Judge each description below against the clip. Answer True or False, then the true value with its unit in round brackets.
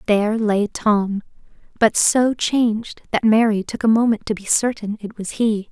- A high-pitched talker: True (215 Hz)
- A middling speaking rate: True (180 wpm)